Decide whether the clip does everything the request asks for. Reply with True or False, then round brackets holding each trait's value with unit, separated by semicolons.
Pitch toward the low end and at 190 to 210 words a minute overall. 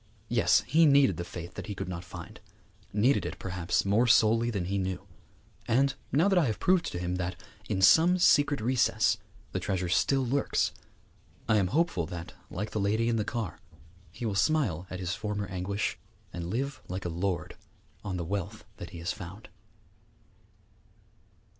False (100 Hz; 180 wpm)